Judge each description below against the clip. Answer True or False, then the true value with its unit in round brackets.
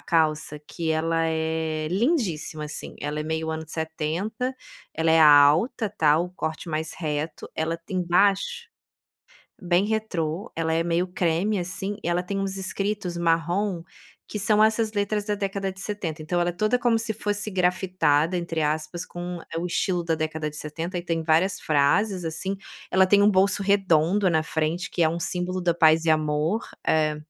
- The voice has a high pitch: False (175 Hz)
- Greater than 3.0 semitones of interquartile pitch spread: True (3.6 semitones)